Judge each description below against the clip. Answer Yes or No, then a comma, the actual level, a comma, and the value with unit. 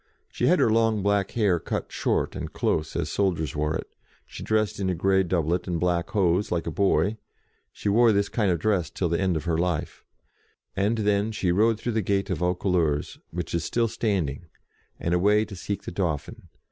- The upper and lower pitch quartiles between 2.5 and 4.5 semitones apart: Yes, average, 3.4 semitones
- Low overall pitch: Yes, very low, 95 Hz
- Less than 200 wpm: No, fast, 205 wpm